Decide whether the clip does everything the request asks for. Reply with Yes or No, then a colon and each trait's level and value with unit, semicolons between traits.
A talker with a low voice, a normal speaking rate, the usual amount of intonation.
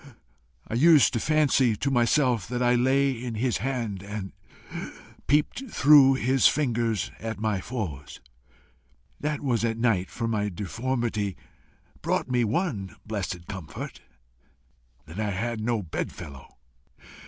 No: low, 115 Hz; slow, 130 wpm; average, 4.1 semitones